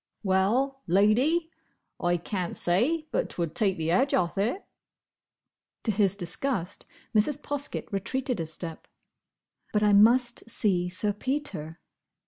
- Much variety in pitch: Yes, wide, 6.6 semitones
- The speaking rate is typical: No, slow, 125 wpm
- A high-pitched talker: Yes, high, 205 Hz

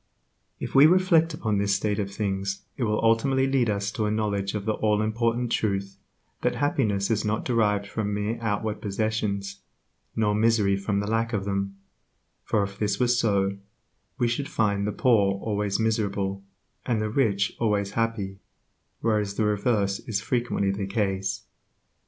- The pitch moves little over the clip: Yes, narrow, 2.3 semitones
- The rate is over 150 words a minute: Yes, average, 165 wpm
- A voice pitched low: Yes, low, 105 Hz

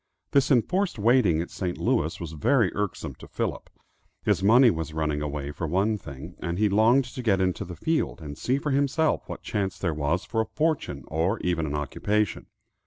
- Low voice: Yes, very low, 95 Hz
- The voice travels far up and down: Yes, wide, 6.9 semitones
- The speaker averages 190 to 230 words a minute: Yes, average, 195 wpm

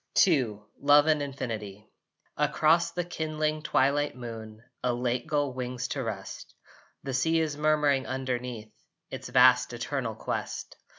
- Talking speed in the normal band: No, slow, 130 wpm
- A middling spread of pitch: Yes, average, 3.6 semitones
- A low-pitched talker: Yes, low, 130 Hz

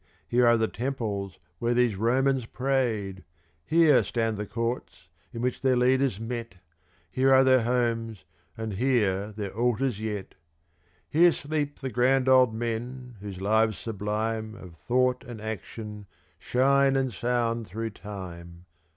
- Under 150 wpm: Yes, average, 140 wpm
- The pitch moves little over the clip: No, average, 3.4 semitones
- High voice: No, low, 115 Hz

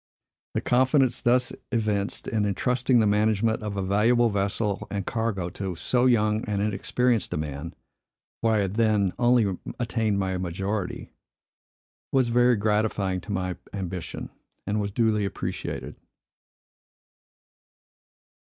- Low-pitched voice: Yes, low, 105 Hz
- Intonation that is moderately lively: Yes, average, 3.0 semitones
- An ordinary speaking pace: No, slow, 125 wpm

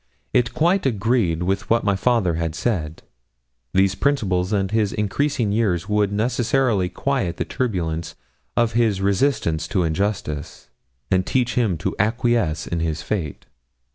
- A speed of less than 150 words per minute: Yes, average, 140 wpm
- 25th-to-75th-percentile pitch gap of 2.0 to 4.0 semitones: No, average, 5.3 semitones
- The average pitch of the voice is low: Yes, low, 100 Hz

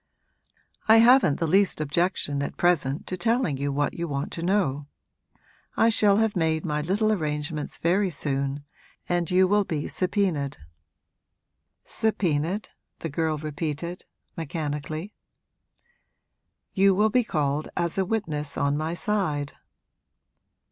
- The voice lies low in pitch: No, medium, 165 Hz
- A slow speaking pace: Yes, slow, 125 wpm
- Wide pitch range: No, average, 5.0 semitones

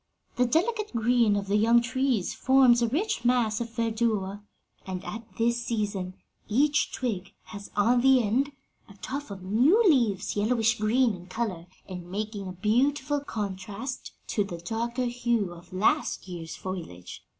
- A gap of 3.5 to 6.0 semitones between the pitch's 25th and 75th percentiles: Yes, average, 4.0 semitones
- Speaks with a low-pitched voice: No, high, 225 Hz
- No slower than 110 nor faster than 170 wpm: Yes, average, 155 wpm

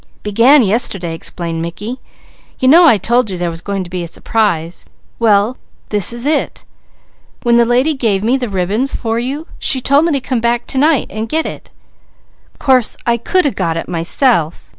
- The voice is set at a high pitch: Yes, high, 230 Hz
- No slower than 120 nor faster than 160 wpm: No, average, 190 wpm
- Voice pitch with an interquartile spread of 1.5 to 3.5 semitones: No, wide, 5.4 semitones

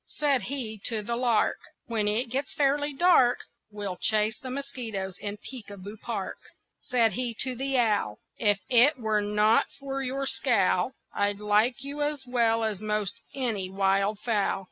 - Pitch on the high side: Yes, high, 230 Hz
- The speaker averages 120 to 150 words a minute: No, average, 165 wpm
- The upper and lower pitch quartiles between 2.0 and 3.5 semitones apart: No, average, 4.0 semitones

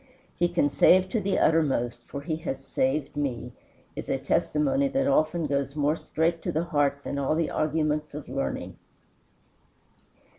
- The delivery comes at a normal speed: Yes, average, 160 wpm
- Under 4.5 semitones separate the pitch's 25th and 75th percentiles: Yes, average, 3.3 semitones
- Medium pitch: Yes, medium, 155 Hz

